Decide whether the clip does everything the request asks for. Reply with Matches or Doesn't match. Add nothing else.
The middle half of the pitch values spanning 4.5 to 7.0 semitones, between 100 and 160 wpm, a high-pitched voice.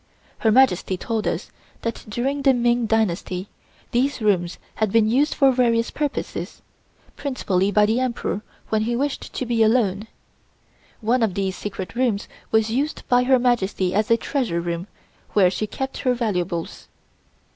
Doesn't match